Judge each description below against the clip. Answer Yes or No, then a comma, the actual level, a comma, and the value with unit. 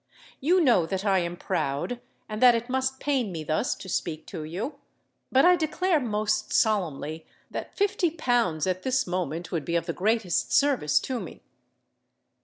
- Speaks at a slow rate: No, average, 175 wpm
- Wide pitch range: Yes, wide, 7.4 semitones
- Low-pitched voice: No, high, 215 Hz